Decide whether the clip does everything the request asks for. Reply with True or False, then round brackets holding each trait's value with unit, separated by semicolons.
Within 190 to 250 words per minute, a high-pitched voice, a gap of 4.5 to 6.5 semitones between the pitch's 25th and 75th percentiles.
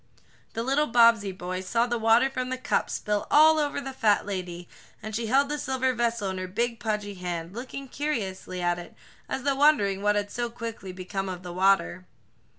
True (200 wpm; 220 Hz; 5.3 semitones)